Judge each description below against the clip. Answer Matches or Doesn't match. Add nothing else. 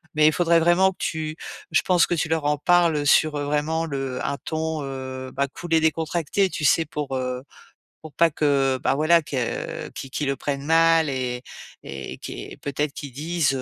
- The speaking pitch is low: Doesn't match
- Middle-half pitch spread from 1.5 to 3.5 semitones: Matches